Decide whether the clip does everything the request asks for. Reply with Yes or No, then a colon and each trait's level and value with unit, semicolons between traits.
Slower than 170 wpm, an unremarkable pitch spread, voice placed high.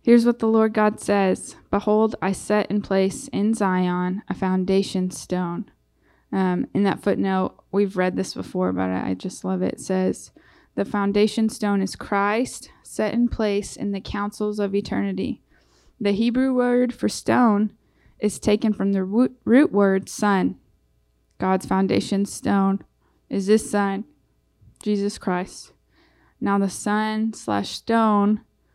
No: average, 145 wpm; narrow, 2.2 semitones; high, 200 Hz